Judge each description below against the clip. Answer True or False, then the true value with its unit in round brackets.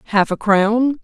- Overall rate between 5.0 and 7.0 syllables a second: False (4.1 syllables/s)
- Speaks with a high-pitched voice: True (220 Hz)